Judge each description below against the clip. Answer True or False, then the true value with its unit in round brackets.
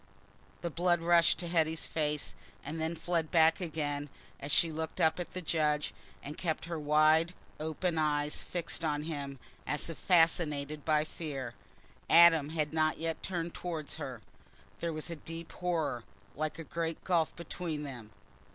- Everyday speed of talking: True (160 wpm)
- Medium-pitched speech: True (160 Hz)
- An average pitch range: False (1.9 semitones)